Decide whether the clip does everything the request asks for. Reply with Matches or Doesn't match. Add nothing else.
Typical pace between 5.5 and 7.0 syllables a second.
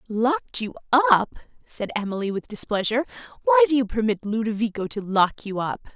Matches